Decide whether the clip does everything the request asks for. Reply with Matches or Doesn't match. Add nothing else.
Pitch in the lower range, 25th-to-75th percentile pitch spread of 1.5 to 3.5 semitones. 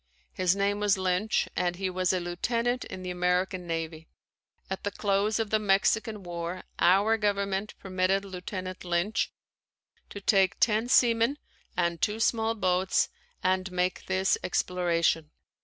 Doesn't match